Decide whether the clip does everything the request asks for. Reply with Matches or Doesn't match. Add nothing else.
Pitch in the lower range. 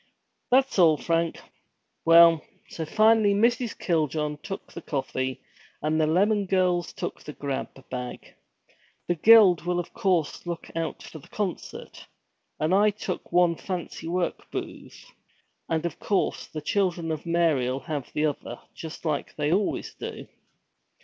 Doesn't match